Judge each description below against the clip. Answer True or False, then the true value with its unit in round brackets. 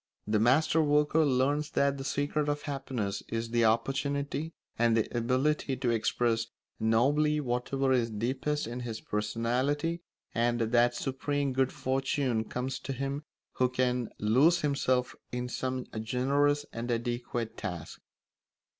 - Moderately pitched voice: False (130 Hz)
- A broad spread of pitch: False (3.4 semitones)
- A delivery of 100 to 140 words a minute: True (135 wpm)